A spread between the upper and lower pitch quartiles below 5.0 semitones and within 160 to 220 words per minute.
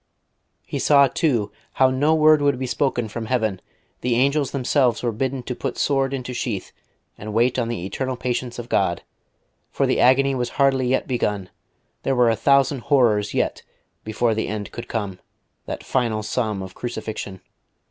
Yes: average, 3.4 semitones; average, 175 wpm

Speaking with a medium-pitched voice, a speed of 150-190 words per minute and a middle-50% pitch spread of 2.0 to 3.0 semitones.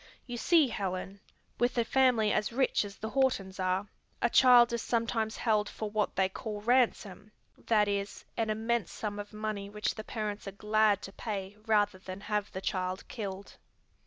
No: high, 210 Hz; average, 180 wpm; narrow, 2.4 semitones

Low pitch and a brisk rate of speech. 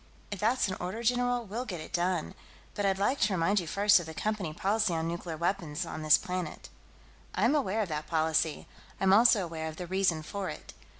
No: medium, 185 Hz; fast, 215 wpm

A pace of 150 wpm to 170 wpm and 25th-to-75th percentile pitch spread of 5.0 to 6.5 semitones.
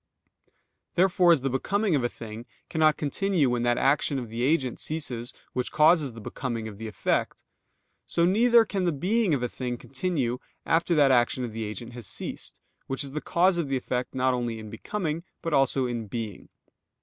No: average, 195 wpm; wide, 5.6 semitones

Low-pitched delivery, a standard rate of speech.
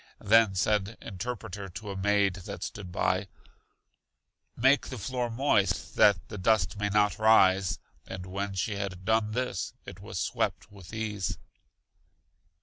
Yes: low, 100 Hz; average, 145 wpm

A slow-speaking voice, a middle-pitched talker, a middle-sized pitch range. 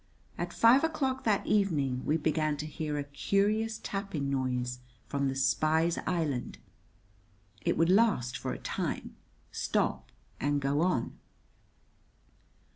No: slow, 125 wpm; medium, 155 Hz; wide, 6.2 semitones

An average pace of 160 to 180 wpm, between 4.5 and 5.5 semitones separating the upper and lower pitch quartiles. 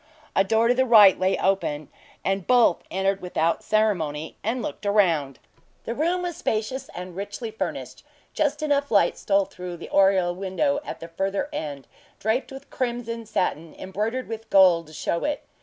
Yes: average, 170 wpm; average, 4.9 semitones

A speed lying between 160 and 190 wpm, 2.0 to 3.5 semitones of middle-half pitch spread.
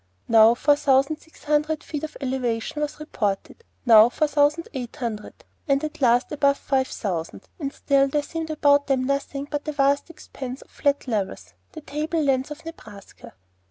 Yes: average, 170 wpm; average, 3.1 semitones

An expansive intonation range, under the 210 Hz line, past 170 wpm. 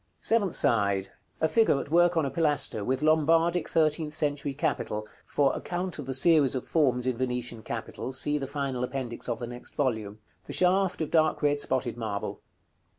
No: average, 4.4 semitones; medium, 140 Hz; average, 180 wpm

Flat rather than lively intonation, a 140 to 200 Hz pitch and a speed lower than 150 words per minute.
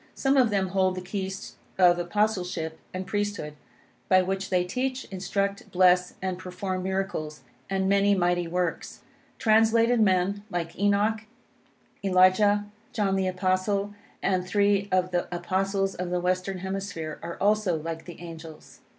Yes: narrow, 2.0 semitones; high, 190 Hz; average, 140 wpm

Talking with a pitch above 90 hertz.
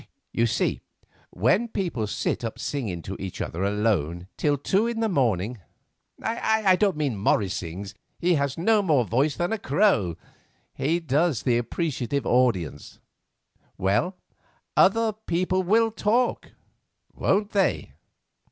Yes: medium, 140 Hz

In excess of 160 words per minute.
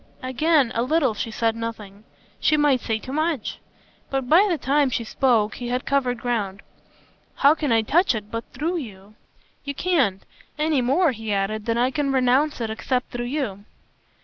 Yes: average, 180 wpm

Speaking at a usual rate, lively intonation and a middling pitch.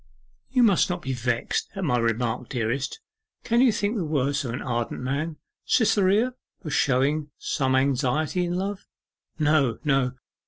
Yes: average, 155 wpm; wide, 6.3 semitones; medium, 145 Hz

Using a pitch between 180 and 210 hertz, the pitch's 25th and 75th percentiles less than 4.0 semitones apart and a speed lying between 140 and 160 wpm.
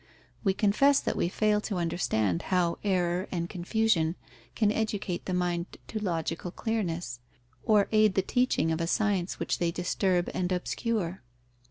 Yes: medium, 185 Hz; average, 3.6 semitones; average, 155 wpm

